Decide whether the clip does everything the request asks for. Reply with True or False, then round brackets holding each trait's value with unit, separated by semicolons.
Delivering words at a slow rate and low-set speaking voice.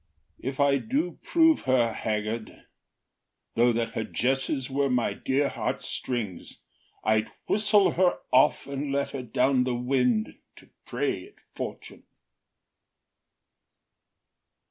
True (115 wpm; 130 Hz)